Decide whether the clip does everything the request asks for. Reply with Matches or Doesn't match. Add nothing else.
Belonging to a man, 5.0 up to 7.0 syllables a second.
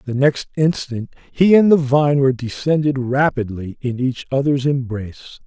Doesn't match